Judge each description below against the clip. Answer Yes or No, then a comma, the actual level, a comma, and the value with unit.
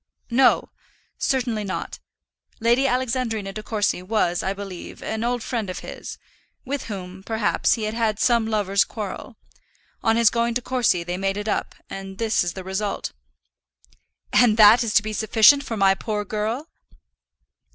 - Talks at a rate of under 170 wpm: Yes, average, 160 wpm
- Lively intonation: No, average, 3.1 semitones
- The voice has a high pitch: Yes, high, 215 Hz